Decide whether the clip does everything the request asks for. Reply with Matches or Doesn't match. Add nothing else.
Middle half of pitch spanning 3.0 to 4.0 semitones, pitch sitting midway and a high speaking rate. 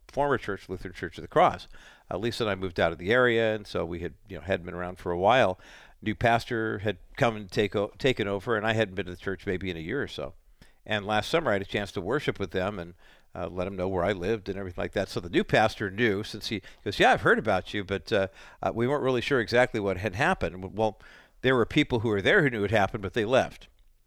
Doesn't match